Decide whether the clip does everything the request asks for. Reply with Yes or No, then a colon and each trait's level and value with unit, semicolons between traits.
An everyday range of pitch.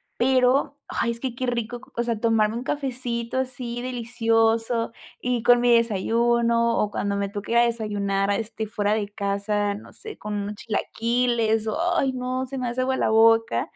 No: narrow, 2.3 semitones